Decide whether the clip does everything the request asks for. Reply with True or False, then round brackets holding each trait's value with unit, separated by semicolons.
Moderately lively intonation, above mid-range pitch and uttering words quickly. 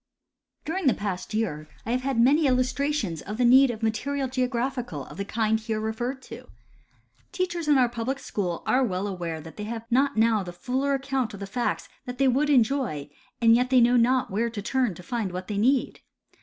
True (4.1 semitones; 240 Hz; 215 wpm)